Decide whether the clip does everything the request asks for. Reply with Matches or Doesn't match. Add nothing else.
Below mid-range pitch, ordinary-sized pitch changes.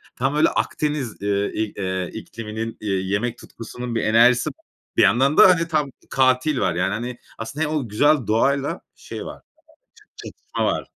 Matches